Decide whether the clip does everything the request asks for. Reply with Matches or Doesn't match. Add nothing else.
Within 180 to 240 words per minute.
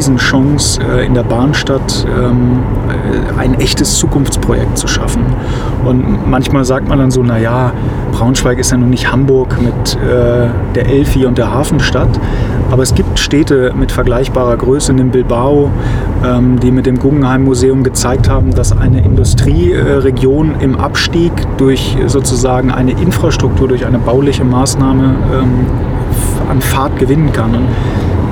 Doesn't match